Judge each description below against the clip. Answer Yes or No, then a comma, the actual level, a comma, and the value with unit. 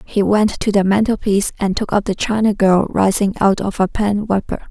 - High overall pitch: Yes, high, 200 Hz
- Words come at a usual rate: No, fast, 230 wpm